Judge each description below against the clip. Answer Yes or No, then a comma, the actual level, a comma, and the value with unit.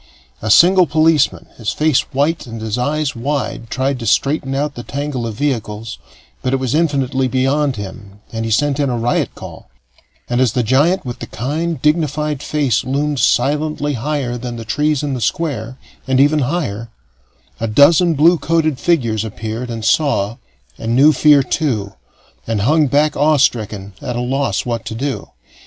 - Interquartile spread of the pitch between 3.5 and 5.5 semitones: Yes, average, 4.4 semitones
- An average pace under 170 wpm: No, average, 175 wpm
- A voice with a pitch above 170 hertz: No, low, 135 Hz